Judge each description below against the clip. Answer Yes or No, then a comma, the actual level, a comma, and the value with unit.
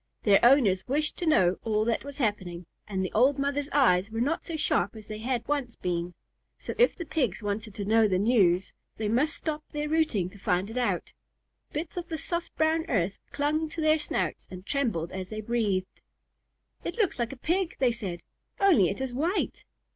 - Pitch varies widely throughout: Yes, wide, 7.1 semitones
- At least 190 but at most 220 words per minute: Yes, average, 200 wpm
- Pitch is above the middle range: Yes, high, 235 Hz